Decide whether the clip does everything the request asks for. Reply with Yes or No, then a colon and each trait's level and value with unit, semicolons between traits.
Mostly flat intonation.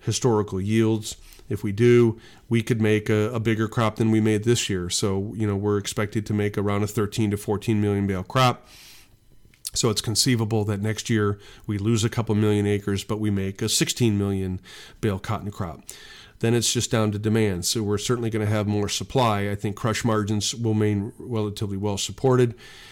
Yes: narrow, 1.7 semitones